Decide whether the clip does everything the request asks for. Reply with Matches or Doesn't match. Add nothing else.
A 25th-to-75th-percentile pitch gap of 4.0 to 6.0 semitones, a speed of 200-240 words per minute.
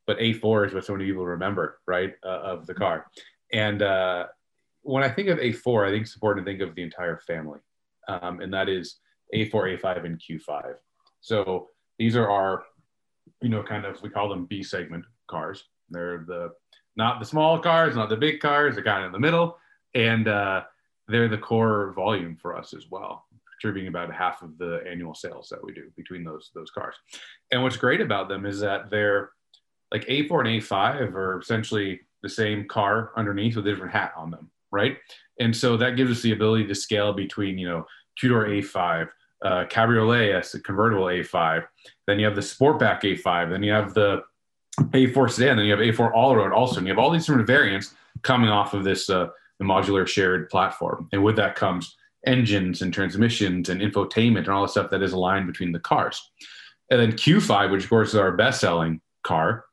Doesn't match